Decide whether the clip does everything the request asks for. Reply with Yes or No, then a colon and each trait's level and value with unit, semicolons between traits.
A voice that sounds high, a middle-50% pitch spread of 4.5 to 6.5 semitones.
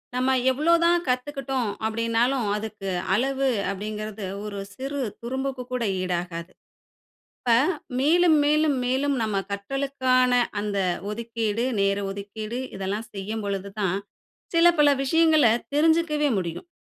Yes: high, 240 Hz; average, 5.1 semitones